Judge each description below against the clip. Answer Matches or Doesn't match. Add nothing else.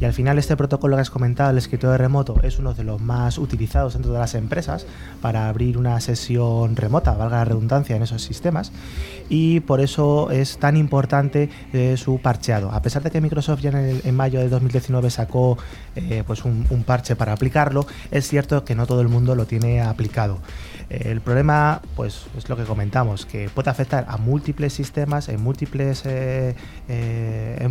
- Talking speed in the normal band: Doesn't match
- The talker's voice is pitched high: Doesn't match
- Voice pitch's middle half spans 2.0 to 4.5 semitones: Matches